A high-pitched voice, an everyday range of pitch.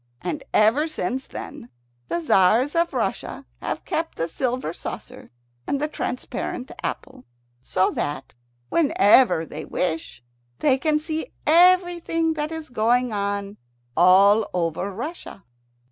No: very high, 250 Hz; wide, 8.2 semitones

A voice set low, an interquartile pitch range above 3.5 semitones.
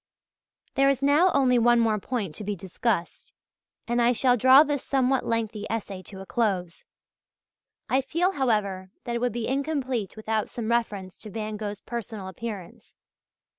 No: high, 230 Hz; average, 3.9 semitones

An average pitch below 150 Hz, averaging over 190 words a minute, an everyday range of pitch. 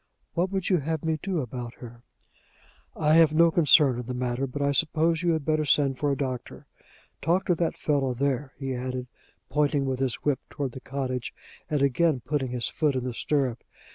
Yes: medium, 140 Hz; average, 200 wpm; average, 3.5 semitones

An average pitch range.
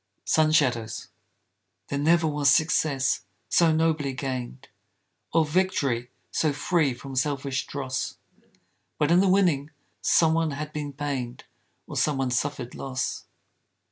Yes: average, 3.1 semitones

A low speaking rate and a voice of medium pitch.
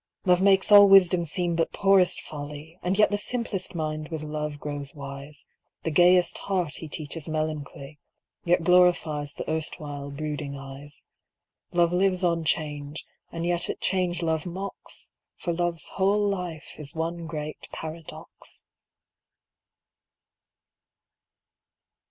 Yes: slow, 130 wpm; medium, 165 Hz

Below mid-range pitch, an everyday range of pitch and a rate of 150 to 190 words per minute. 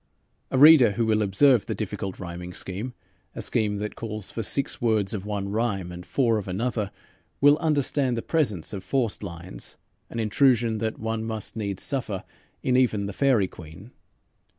Yes: low, 110 Hz; average, 4.0 semitones; average, 175 wpm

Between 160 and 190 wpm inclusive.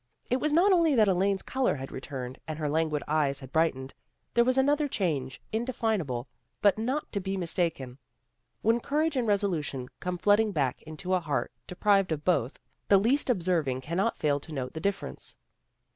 Yes: average, 180 wpm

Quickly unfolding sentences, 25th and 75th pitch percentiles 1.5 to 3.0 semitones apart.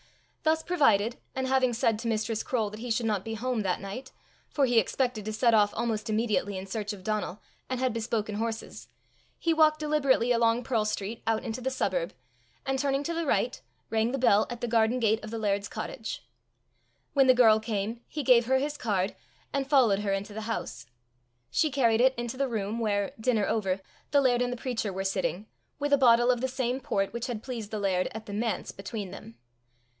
No: fast, 210 wpm; average, 3.4 semitones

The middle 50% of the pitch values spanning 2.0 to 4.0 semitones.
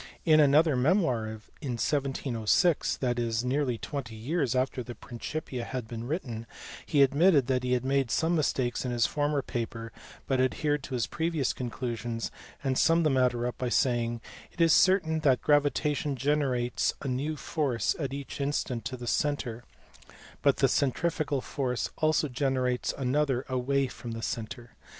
Yes: average, 3.3 semitones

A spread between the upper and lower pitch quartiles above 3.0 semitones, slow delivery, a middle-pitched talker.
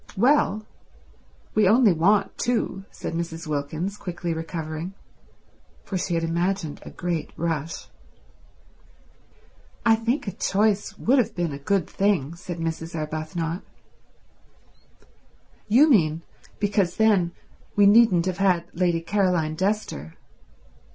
Yes: average, 3.8 semitones; slow, 115 wpm; medium, 180 Hz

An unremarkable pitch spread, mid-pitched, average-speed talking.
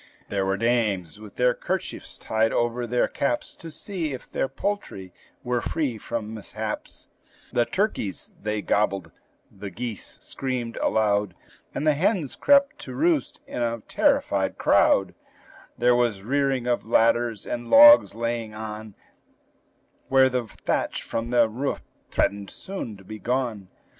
No: average, 3.6 semitones; low, 120 Hz; average, 145 wpm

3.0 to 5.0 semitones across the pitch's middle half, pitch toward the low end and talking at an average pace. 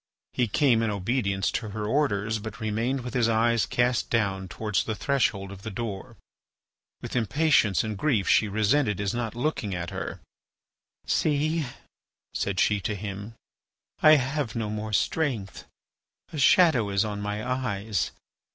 Yes: average, 3.7 semitones; low, 110 Hz; average, 150 wpm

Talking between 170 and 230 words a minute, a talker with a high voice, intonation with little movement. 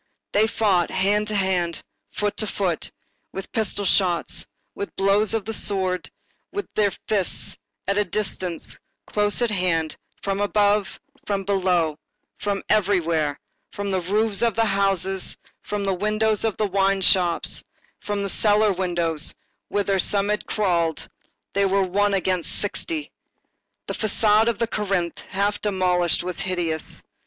No: average, 145 wpm; high, 195 Hz; narrow, 2.3 semitones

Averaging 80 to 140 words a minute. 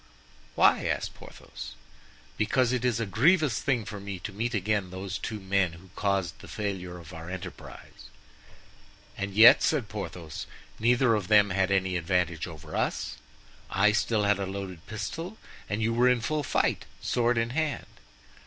No: average, 165 wpm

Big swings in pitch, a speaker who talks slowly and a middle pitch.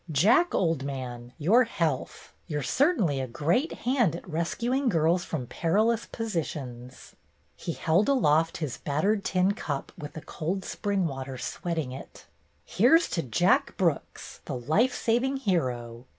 No: wide, 7.5 semitones; average, 145 wpm; medium, 165 Hz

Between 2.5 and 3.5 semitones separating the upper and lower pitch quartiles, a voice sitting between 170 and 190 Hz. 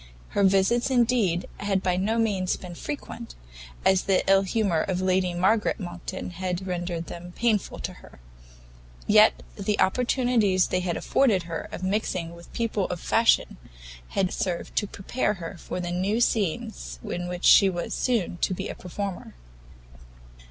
Yes: average, 2.9 semitones; medium, 185 Hz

